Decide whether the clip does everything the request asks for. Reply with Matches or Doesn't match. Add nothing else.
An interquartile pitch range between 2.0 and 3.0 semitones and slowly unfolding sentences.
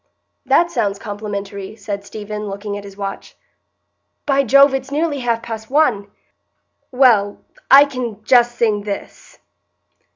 Doesn't match